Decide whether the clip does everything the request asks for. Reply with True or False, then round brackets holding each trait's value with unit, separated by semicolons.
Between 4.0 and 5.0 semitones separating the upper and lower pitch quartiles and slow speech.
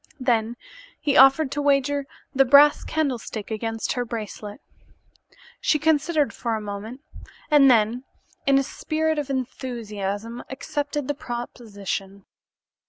True (4.5 semitones; 120 wpm)